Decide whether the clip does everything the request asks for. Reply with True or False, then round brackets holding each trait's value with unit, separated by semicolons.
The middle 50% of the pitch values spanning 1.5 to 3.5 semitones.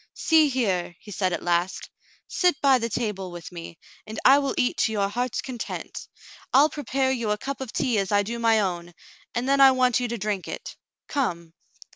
False (5.5 semitones)